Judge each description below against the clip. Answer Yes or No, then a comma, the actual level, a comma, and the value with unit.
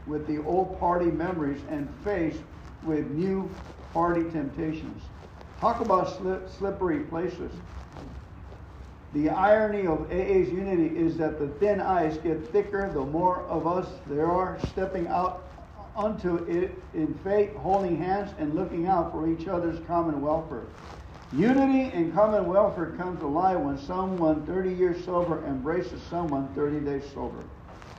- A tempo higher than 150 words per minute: No, average, 145 wpm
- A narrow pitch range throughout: No, average, 3.8 semitones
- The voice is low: No, medium, 170 Hz